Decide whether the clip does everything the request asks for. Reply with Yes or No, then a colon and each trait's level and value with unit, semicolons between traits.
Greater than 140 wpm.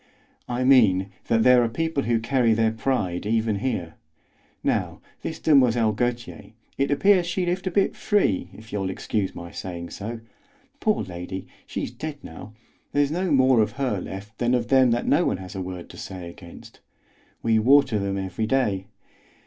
Yes: average, 175 wpm